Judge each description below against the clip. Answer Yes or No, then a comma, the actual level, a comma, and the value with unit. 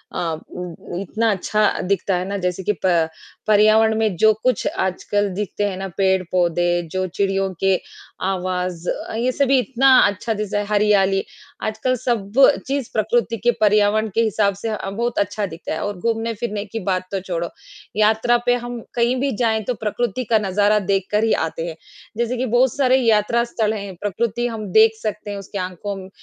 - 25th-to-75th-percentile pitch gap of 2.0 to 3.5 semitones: Yes, average, 3.1 semitones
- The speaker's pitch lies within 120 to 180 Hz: No, high, 210 Hz